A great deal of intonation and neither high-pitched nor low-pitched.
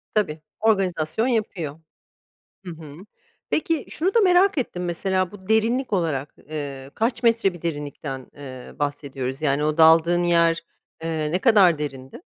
Yes: wide, 6.6 semitones; medium, 170 Hz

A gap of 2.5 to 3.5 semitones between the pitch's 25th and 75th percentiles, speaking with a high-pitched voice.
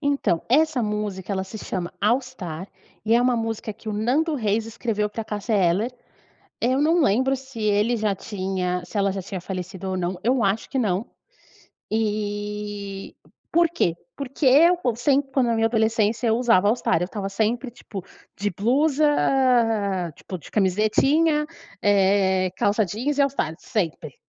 No: average, 4.3 semitones; high, 215 Hz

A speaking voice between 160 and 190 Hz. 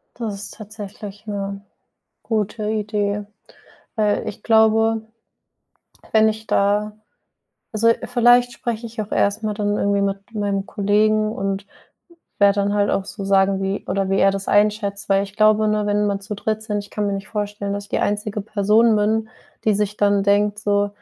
No: high, 205 Hz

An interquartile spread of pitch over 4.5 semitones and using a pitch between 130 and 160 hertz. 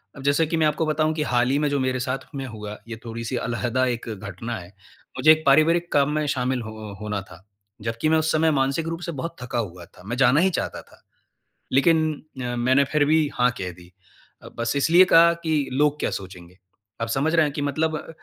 Yes: average, 5.0 semitones; low, 135 Hz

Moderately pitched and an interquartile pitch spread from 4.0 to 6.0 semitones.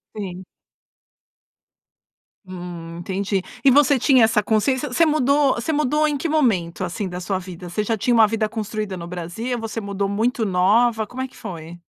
No: high, 215 Hz; average, 5.2 semitones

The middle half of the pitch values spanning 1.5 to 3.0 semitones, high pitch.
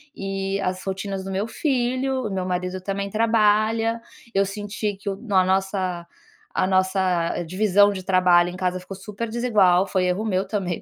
Yes: narrow, 2.4 semitones; high, 195 Hz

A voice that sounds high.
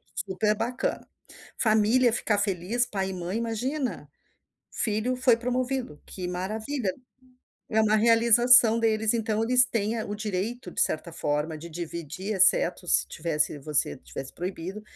Yes: high, 215 Hz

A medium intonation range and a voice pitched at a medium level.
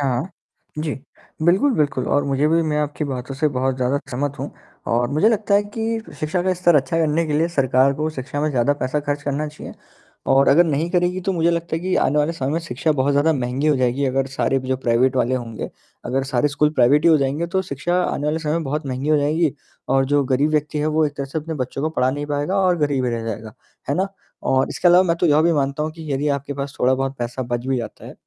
Yes: average, 3.3 semitones; medium, 145 Hz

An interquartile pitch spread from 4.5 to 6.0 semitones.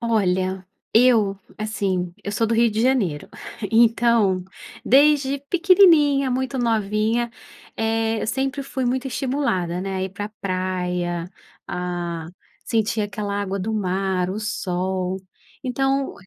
Yes: average, 5.0 semitones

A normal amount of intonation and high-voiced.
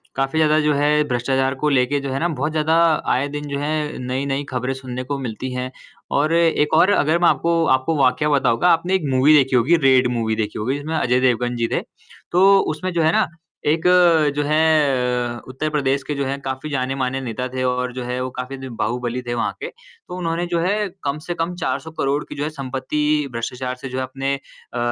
No: average, 3.3 semitones; low, 135 Hz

